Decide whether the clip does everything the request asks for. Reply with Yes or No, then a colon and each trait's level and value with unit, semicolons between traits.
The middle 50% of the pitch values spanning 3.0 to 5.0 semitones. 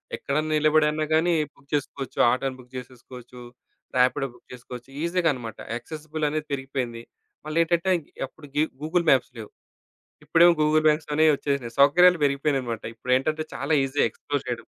Yes: average, 3.5 semitones